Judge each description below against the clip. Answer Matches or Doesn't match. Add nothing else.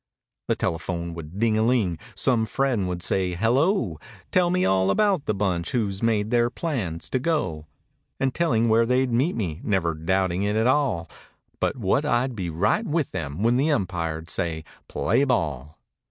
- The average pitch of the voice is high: Doesn't match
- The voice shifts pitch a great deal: Matches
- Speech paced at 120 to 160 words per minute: Doesn't match